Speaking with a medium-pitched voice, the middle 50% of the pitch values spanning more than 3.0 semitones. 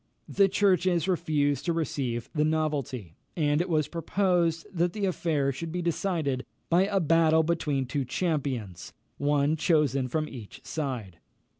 Yes: medium, 155 Hz; average, 3.7 semitones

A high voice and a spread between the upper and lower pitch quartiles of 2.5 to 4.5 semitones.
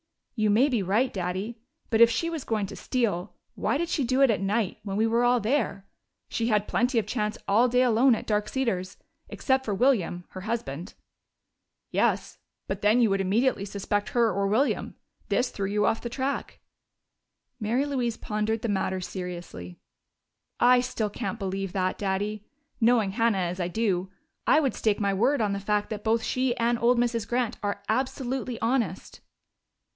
Yes: high, 220 Hz; average, 3.7 semitones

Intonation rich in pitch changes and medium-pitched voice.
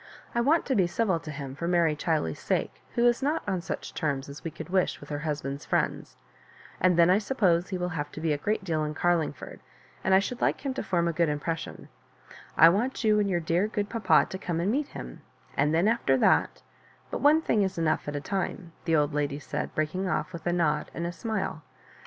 No: average, 4.7 semitones; medium, 175 Hz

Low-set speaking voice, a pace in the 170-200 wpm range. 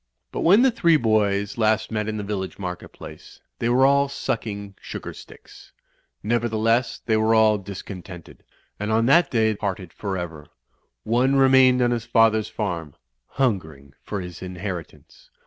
No: low, 110 Hz; average, 155 wpm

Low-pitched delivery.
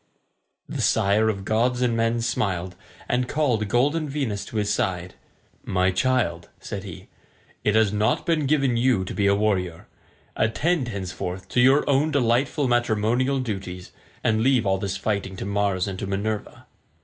Yes: low, 110 Hz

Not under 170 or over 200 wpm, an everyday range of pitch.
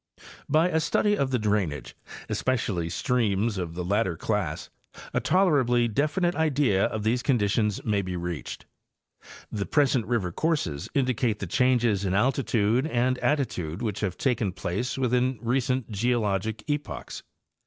No: average, 140 wpm; average, 4.7 semitones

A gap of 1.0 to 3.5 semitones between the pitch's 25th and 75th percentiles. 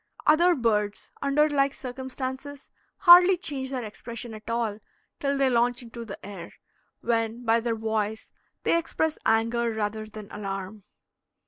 No: average, 4.0 semitones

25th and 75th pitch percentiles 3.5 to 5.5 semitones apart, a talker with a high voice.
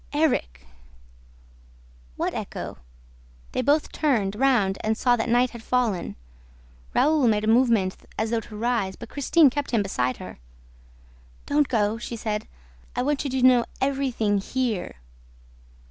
Yes: average, 3.8 semitones; high, 235 Hz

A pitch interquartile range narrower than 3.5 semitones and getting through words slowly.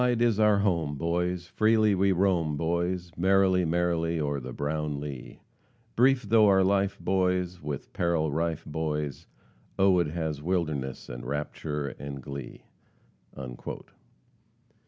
No: average, 4.3 semitones; slow, 130 wpm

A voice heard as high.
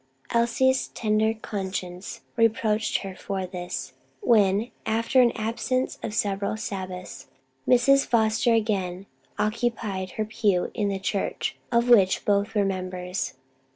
Yes: high, 210 Hz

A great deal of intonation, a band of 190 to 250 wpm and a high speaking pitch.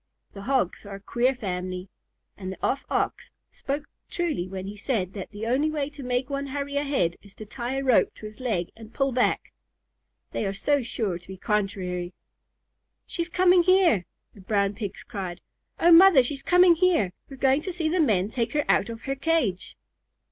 Yes: wide, 6.6 semitones; average, 195 wpm; high, 245 Hz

